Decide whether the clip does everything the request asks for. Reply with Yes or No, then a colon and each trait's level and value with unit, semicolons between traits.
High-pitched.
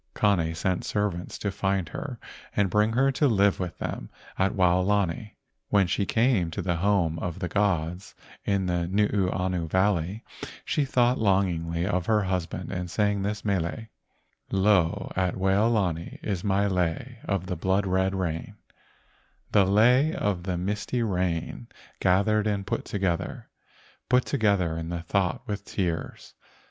No: very low, 95 Hz